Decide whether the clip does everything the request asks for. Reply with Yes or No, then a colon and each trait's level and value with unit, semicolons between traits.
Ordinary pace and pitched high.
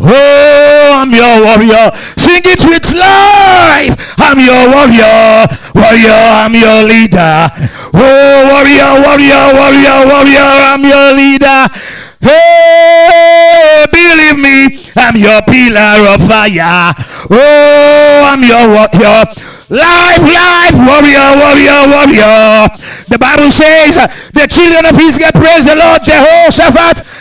No: slow, 115 wpm; very high, 280 Hz